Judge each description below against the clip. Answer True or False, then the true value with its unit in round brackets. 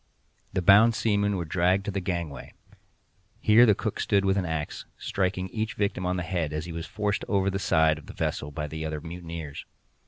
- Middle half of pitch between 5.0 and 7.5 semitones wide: False (3.7 semitones)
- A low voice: True (90 Hz)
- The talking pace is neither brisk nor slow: False (210 wpm)